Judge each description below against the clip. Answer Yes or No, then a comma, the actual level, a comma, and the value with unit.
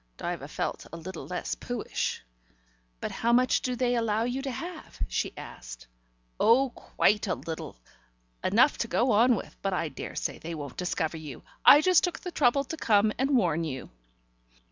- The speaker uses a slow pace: No, average, 175 wpm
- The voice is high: Yes, high, 215 Hz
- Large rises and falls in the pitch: Yes, wide, 7.4 semitones